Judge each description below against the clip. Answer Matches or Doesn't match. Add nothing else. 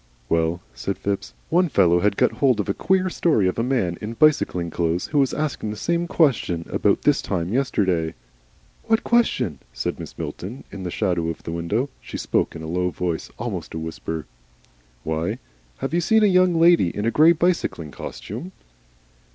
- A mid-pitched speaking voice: Doesn't match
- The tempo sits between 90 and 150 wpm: Doesn't match